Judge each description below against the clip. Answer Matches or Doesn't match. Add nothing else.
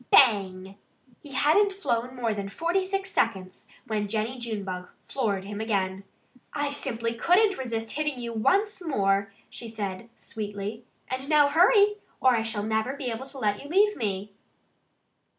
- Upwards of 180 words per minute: Doesn't match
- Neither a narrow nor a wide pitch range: Doesn't match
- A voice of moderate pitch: Doesn't match